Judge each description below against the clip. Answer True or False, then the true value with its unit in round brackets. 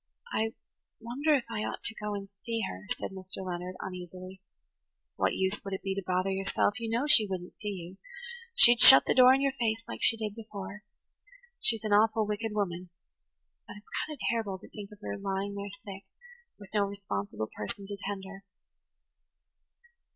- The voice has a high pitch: True (205 Hz)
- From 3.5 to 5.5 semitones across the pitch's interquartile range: False (2.9 semitones)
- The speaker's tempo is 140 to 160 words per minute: False (180 wpm)